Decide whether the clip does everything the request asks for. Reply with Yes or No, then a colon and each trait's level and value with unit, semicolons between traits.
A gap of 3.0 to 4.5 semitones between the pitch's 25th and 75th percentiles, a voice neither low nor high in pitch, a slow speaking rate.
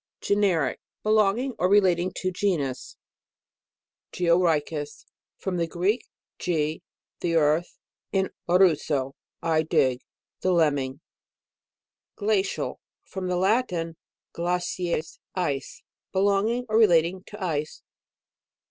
Yes: average, 3.5 semitones; medium, 175 Hz; slow, 110 wpm